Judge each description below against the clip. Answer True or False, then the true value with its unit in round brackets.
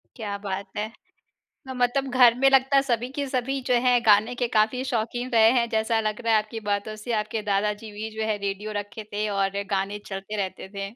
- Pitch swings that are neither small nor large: True (3.1 semitones)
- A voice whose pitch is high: True (220 Hz)